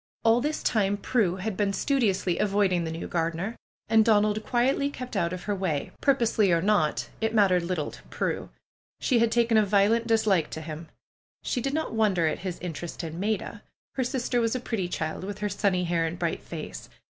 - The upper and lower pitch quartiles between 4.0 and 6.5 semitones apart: Yes, average, 4.5 semitones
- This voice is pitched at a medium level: No, high, 200 Hz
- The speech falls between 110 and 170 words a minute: No, average, 200 wpm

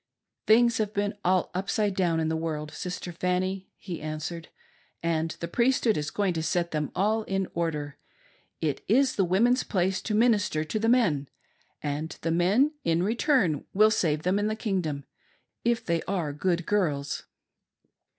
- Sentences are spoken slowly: No, average, 170 wpm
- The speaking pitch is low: No, medium, 180 Hz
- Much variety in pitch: No, average, 4.7 semitones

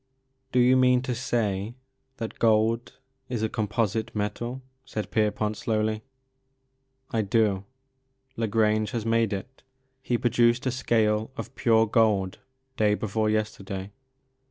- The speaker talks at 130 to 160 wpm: Yes, average, 150 wpm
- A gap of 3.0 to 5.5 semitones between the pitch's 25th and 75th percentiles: No, narrow, 2.6 semitones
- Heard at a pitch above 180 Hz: No, low, 110 Hz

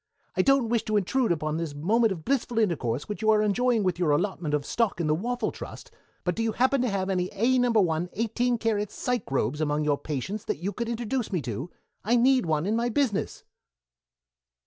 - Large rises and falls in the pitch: Yes, wide, 6.2 semitones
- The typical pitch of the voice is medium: No, high, 210 Hz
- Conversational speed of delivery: No, fast, 215 wpm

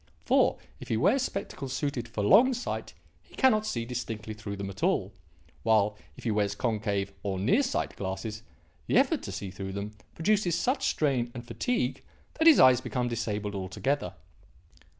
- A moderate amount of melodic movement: No, wide, 7.3 semitones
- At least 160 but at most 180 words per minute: Yes, average, 170 wpm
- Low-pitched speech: Yes, low, 115 Hz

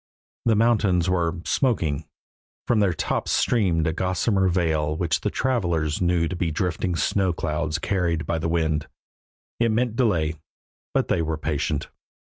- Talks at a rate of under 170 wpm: Yes, average, 150 wpm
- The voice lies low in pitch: Yes, very low, 85 Hz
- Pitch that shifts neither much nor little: Yes, average, 3.6 semitones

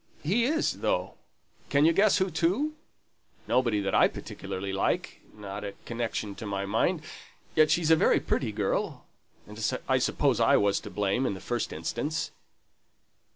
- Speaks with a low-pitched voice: Yes, low, 120 Hz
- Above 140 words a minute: Yes, average, 160 wpm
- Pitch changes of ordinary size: No, wide, 8.4 semitones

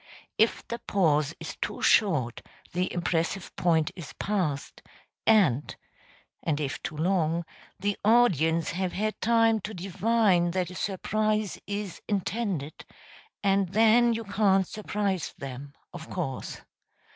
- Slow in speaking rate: Yes, slow, 125 wpm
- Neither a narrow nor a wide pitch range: Yes, average, 4.6 semitones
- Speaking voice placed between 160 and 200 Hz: Yes, high, 190 Hz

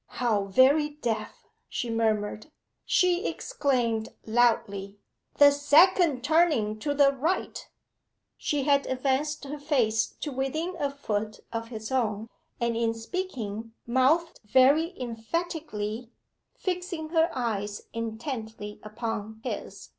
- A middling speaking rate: No, slow, 115 wpm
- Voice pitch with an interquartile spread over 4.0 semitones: Yes, average, 5.1 semitones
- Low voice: No, very high, 250 Hz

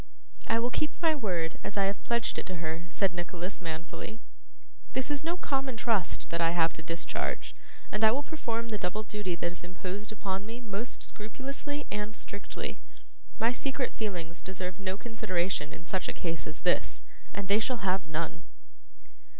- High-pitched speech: Yes, high, 200 Hz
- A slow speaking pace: No, average, 180 wpm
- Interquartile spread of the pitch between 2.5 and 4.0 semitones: No, average, 4.7 semitones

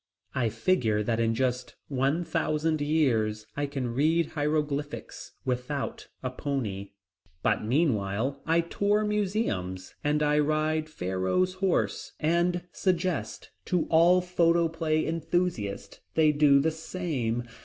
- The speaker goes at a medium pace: No, slow, 120 wpm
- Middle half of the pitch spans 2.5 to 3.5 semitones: No, average, 5.2 semitones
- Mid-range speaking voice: Yes, medium, 150 Hz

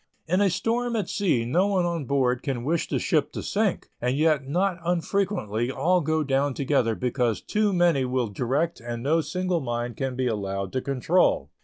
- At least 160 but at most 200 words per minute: Yes, average, 190 wpm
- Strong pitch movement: Yes, wide, 6.2 semitones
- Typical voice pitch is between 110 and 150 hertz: Yes, medium, 140 Hz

